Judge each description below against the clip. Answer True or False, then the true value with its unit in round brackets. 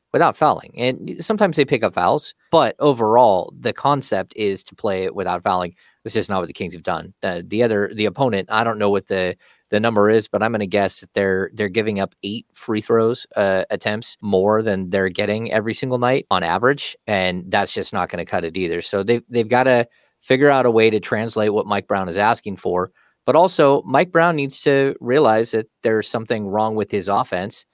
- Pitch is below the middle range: True (110 Hz)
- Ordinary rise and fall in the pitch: True (3.3 semitones)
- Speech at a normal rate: False (225 wpm)